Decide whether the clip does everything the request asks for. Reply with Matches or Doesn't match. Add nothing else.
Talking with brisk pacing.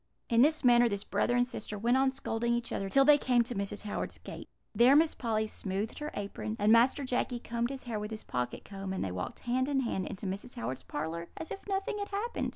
Matches